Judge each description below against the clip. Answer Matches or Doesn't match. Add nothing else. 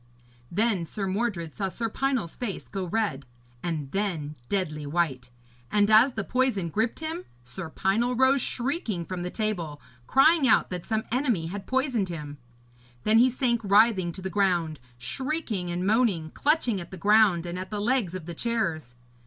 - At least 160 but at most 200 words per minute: Matches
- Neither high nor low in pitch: Doesn't match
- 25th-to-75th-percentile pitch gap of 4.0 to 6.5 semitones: Matches